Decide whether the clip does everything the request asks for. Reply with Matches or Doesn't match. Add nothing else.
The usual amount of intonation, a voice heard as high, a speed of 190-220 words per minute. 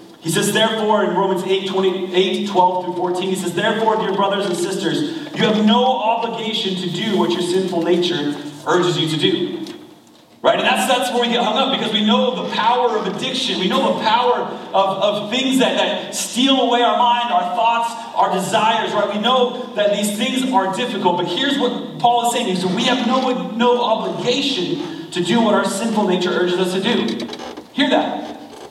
Matches